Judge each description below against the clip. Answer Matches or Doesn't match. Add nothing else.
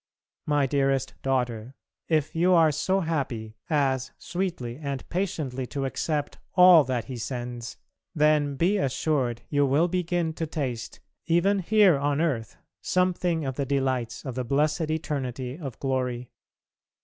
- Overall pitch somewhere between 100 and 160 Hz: Matches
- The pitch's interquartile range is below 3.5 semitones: Doesn't match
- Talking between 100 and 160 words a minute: Matches